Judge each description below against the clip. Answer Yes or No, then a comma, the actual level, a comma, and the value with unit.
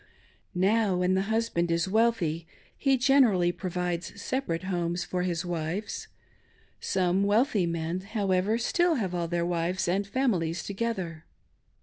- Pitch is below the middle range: No, medium, 185 Hz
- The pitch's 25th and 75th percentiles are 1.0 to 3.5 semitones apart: No, average, 4.0 semitones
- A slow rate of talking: Yes, slow, 130 wpm